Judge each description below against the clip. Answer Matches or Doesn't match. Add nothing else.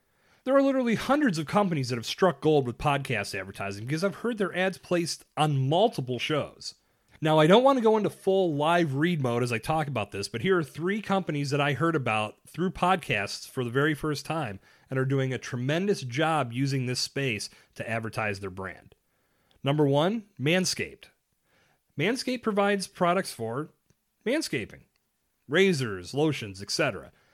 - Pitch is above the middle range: Doesn't match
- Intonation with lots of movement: Matches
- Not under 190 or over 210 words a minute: Doesn't match